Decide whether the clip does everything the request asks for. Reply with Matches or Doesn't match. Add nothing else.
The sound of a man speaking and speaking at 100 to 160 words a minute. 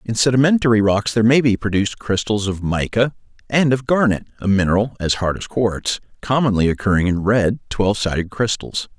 Doesn't match